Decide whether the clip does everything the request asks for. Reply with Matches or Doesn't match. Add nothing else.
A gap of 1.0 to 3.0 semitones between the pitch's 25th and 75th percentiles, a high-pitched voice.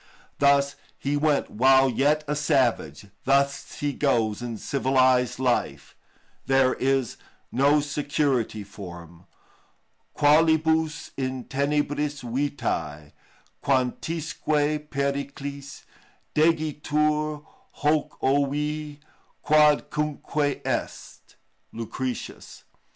Doesn't match